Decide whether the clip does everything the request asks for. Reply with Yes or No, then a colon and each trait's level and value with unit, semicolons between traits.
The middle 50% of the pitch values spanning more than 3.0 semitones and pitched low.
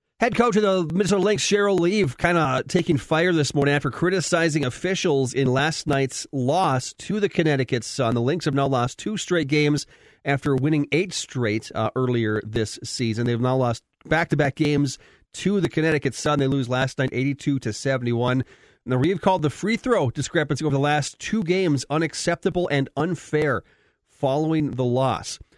No: average, 4.7 semitones; medium, 145 Hz